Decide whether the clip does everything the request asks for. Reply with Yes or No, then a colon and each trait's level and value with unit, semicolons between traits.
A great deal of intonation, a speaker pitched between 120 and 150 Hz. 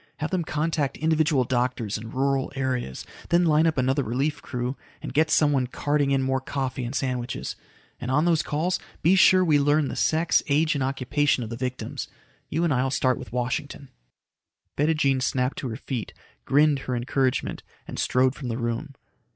No: average, 3.0 semitones; low, 135 Hz